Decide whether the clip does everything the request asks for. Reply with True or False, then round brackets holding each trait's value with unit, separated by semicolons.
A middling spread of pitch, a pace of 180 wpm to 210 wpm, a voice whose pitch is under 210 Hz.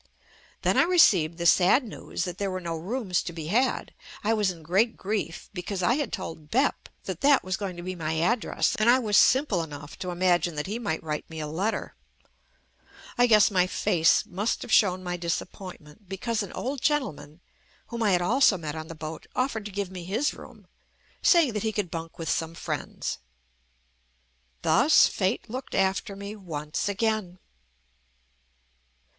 True (4.7 semitones; 185 wpm; 190 Hz)